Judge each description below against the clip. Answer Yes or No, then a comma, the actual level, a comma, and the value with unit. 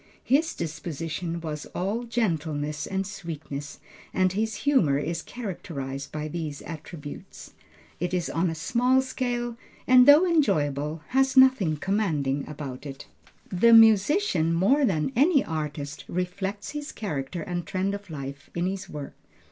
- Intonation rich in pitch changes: Yes, wide, 7.0 semitones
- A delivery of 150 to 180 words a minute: No, average, 140 wpm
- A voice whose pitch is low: No, medium, 175 Hz